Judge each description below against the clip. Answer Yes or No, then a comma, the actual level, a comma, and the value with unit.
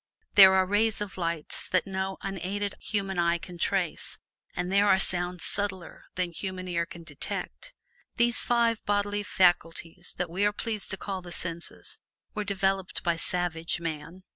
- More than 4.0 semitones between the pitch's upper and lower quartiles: No, average, 2.7 semitones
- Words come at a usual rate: Yes, average, 165 wpm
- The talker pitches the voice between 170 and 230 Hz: Yes, medium, 185 Hz